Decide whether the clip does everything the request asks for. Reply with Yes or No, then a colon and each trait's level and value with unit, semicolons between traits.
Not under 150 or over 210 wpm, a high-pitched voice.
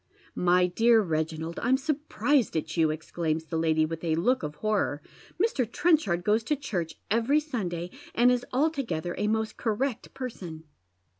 Yes: average, 165 wpm; high, 210 Hz